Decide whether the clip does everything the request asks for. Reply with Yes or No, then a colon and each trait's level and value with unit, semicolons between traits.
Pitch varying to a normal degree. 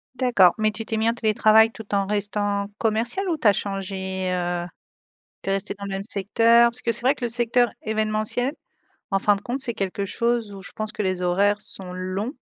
Yes: average, 3.1 semitones